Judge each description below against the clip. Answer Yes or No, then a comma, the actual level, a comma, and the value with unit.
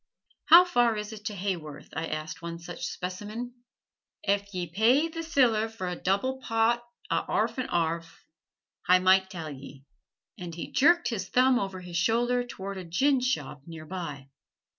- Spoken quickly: No, average, 165 wpm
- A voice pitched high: Yes, high, 195 Hz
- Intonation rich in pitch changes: Yes, wide, 6.1 semitones